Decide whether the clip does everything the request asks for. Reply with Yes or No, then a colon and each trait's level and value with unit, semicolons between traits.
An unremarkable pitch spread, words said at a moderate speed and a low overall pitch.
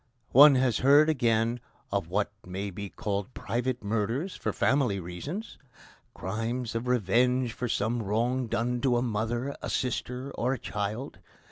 Yes: average, 3.3 semitones; average, 150 wpm; low, 120 Hz